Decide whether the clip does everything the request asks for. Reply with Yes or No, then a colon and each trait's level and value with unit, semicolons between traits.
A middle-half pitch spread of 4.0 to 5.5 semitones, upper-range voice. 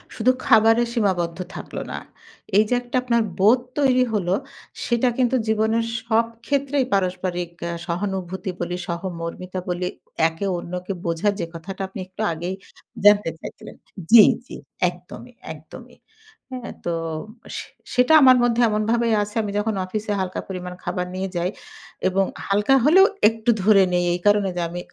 Yes: average, 4.3 semitones; high, 200 Hz